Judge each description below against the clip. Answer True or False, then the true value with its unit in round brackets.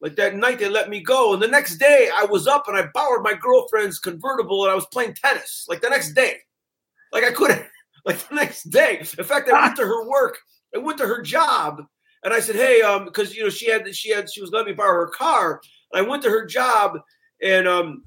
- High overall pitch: True (270 Hz)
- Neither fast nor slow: False (250 wpm)